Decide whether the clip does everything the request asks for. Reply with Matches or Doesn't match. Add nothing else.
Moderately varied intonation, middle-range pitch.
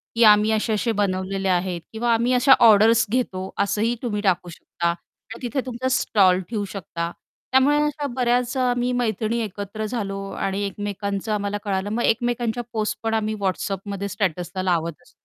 Doesn't match